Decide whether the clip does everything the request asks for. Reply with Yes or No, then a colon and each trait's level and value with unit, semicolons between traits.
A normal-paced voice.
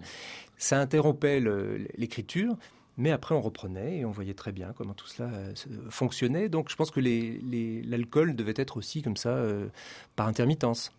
Yes: average, 175 wpm